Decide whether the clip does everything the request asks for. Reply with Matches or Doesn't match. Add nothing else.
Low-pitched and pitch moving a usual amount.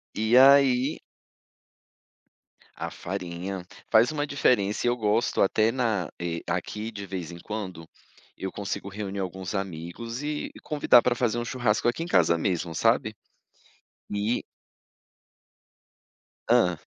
Matches